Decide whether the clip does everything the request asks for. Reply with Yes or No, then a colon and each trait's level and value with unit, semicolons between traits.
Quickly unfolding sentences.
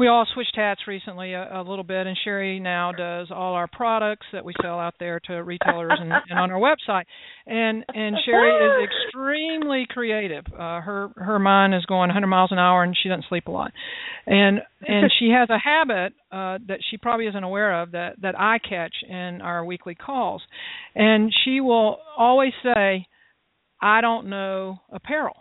No: average, 190 wpm